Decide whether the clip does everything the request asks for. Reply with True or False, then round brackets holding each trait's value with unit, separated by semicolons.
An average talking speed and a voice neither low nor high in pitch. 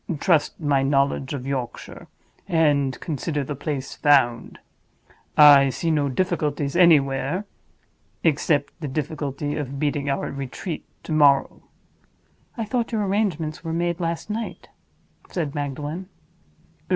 False (120 wpm; 150 Hz)